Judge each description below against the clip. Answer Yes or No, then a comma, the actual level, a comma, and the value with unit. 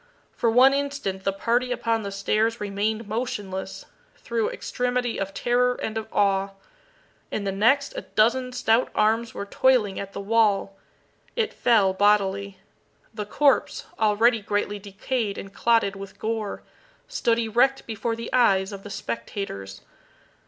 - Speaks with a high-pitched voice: Yes, high, 215 Hz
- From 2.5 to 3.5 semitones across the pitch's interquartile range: Yes, average, 3.2 semitones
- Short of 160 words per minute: Yes, average, 145 wpm